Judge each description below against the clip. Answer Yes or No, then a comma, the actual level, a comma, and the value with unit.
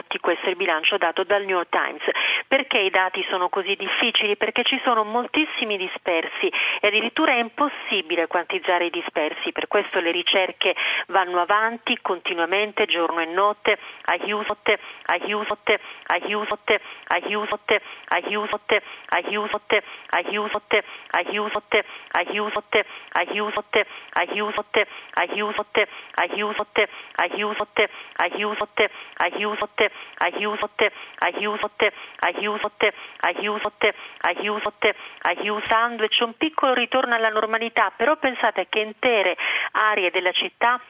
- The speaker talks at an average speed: No, slow, 110 wpm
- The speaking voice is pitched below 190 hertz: No, high, 210 Hz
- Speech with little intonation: Yes, narrow, 1.3 semitones